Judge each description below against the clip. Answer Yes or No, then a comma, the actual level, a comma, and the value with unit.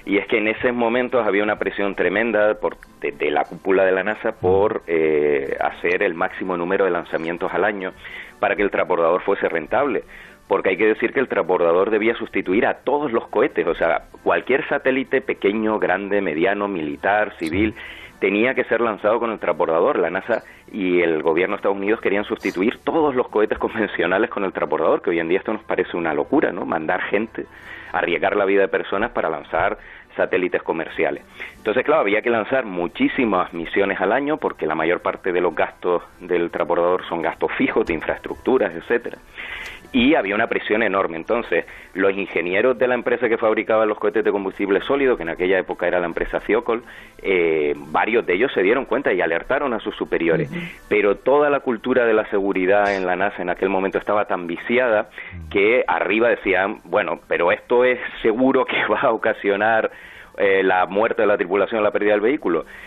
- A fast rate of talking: Yes, fast, 195 wpm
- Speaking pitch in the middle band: No, low, 125 Hz